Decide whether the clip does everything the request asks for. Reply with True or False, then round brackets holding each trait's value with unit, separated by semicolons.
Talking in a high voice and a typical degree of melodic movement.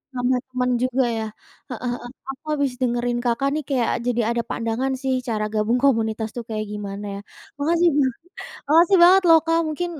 True (250 Hz; 3.6 semitones)